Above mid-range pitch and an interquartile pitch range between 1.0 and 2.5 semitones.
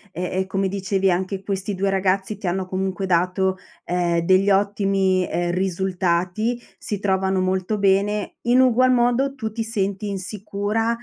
Yes: high, 195 Hz; narrow, 1.8 semitones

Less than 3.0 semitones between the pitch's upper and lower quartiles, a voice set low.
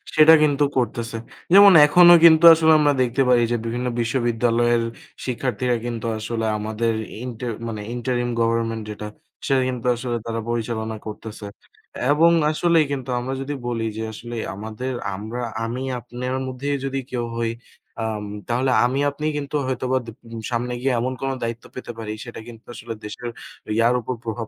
Yes: narrow, 2.4 semitones; low, 120 Hz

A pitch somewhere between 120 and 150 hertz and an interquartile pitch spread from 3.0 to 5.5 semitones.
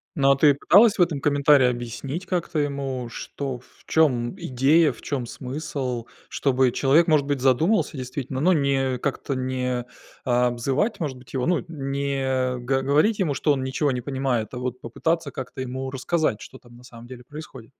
No: low, 135 Hz; narrow, 2.6 semitones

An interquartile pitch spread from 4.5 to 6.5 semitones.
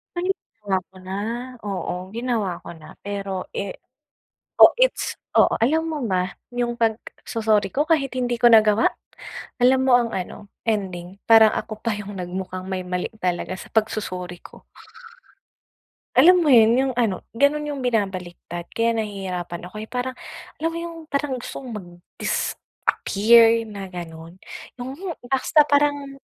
Yes: average, 5.2 semitones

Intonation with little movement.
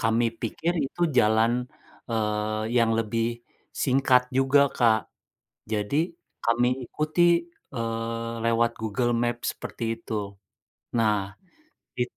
Yes: narrow, 2.1 semitones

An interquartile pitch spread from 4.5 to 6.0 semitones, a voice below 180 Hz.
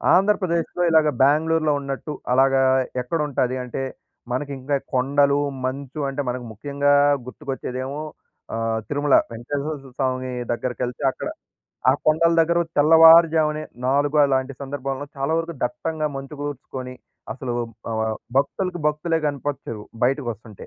No: average, 3.0 semitones; medium, 140 Hz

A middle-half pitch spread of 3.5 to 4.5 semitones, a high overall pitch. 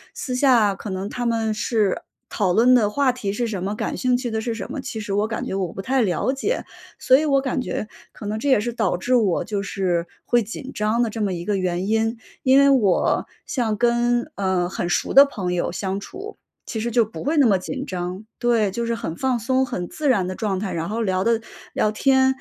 Yes: average, 4.2 semitones; high, 220 Hz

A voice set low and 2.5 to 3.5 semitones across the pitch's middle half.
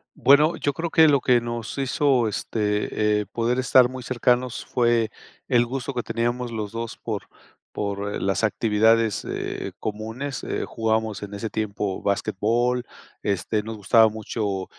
Yes: low, 115 Hz; average, 2.9 semitones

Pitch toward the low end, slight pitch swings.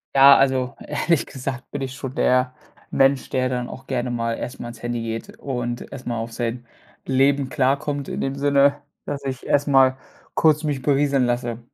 Yes: low, 130 Hz; narrow, 2.3 semitones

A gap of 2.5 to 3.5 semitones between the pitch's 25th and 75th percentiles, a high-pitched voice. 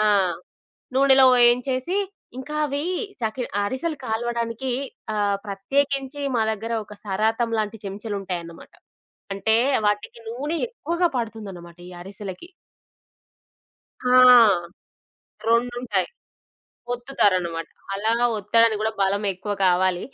No: average, 4.3 semitones; high, 225 Hz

